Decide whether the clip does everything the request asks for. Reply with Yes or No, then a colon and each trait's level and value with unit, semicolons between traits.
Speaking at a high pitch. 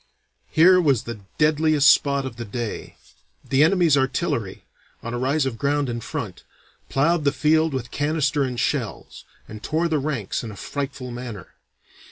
No: medium, 140 Hz